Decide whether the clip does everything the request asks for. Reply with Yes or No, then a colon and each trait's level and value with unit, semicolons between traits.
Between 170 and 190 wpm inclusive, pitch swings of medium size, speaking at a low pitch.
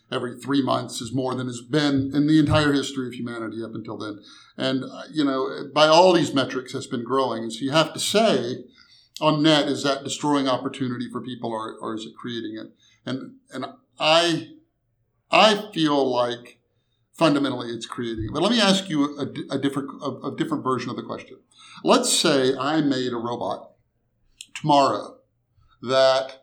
Yes: average, 180 wpm; average, 3.2 semitones; low, 130 Hz